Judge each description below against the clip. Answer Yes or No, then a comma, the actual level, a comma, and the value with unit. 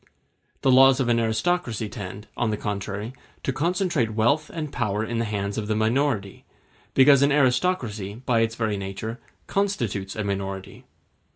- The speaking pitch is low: Yes, low, 115 Hz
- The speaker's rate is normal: Yes, average, 160 wpm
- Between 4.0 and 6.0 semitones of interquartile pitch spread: Yes, average, 4.5 semitones